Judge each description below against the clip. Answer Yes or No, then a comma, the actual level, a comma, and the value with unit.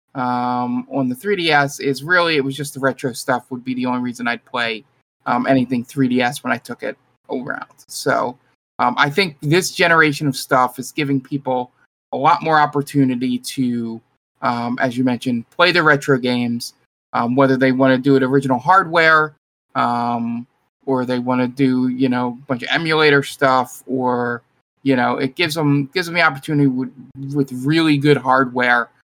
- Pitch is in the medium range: No, low, 130 Hz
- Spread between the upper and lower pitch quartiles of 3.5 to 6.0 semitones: No, narrow, 2.4 semitones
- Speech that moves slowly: No, average, 180 wpm